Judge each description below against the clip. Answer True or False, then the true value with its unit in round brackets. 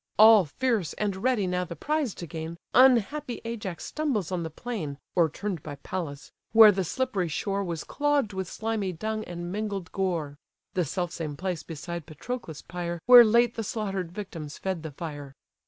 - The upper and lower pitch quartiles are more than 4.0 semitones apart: True (4.8 semitones)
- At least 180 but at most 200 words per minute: False (170 wpm)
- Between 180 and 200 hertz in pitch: True (185 Hz)